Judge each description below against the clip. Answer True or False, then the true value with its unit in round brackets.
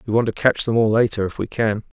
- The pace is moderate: False (300 wpm)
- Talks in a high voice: False (110 Hz)